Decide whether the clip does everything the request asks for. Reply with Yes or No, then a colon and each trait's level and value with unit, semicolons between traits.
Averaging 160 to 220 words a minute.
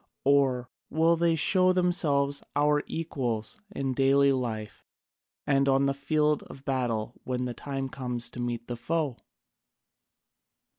No: slow, 135 wpm